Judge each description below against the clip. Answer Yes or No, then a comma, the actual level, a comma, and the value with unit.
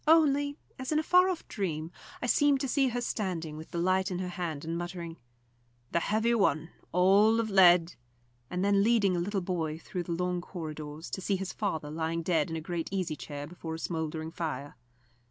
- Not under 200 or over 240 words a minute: Yes, fast, 205 wpm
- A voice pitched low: No, medium, 180 Hz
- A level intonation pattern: No, average, 4.1 semitones